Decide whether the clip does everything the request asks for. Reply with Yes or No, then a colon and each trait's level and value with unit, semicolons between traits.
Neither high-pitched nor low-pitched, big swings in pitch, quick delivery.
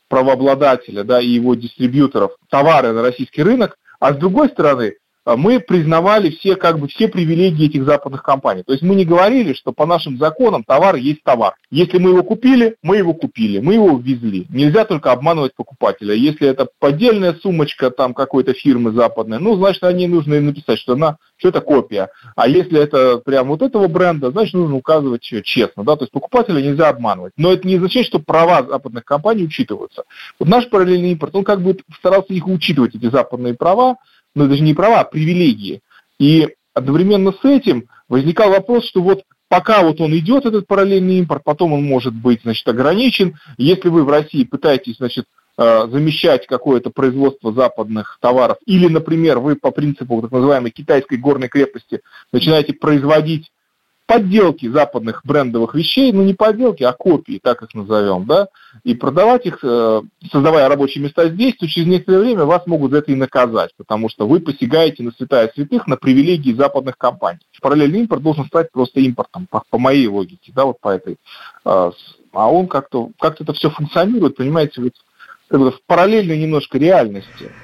Yes: medium, 155 Hz; wide, 5.9 semitones; fast, 175 wpm